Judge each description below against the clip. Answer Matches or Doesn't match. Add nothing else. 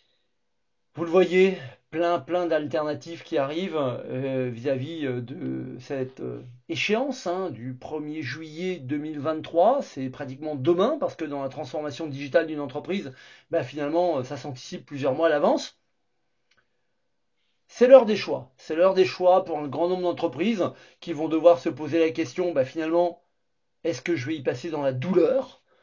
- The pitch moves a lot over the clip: Doesn't match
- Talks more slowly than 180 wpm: Matches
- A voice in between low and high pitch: Matches